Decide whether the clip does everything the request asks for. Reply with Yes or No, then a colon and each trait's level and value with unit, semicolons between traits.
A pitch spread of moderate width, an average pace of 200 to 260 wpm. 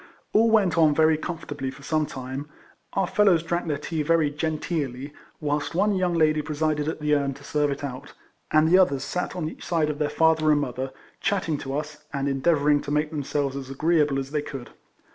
No: narrow, 2.3 semitones; fast, 205 wpm